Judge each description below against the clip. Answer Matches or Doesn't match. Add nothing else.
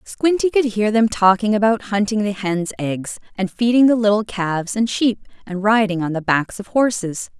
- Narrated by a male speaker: Doesn't match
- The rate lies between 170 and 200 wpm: Matches